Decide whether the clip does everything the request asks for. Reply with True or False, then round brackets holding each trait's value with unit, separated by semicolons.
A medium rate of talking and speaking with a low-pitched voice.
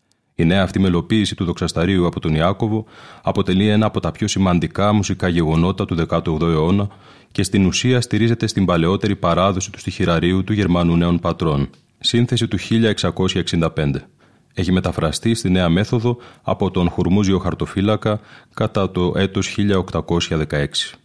True (135 wpm; 95 Hz)